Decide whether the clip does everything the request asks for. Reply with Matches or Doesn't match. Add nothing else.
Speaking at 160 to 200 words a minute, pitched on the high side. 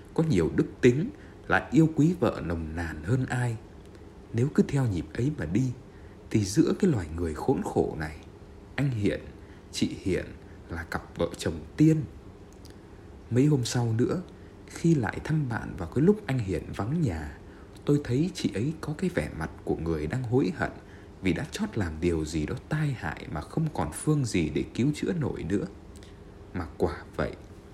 Doesn't match